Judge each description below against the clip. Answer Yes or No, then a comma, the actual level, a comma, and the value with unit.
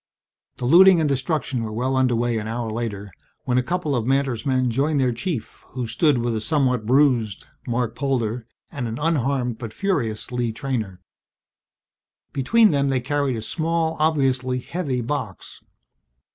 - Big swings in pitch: No, average, 3.5 semitones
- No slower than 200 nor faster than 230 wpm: No, average, 160 wpm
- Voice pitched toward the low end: Yes, low, 130 Hz